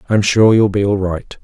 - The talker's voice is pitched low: Yes, low, 100 Hz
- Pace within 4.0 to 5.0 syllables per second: Yes, 4.9 syllables/s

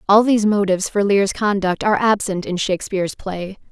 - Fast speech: No, average, 180 wpm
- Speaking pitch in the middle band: No, high, 200 Hz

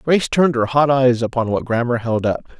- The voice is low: Yes, low, 125 Hz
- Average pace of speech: No, fast, 230 wpm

